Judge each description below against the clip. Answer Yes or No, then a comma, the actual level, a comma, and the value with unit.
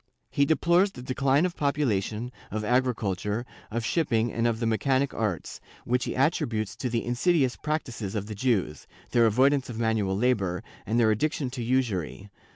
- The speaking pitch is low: Yes, low, 120 Hz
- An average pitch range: Yes, average, 3.7 semitones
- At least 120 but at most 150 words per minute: No, average, 165 wpm